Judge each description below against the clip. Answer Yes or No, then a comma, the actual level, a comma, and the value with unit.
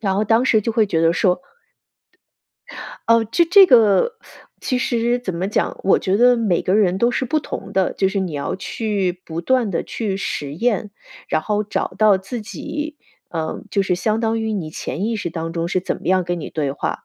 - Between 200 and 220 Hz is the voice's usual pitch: Yes, high, 205 Hz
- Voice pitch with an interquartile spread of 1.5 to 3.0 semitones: No, average, 4.3 semitones